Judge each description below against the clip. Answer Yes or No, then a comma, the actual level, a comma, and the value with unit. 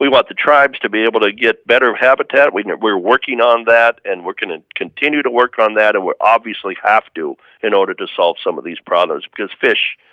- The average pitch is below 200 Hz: Yes, low, 135 Hz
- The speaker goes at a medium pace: No, fast, 230 wpm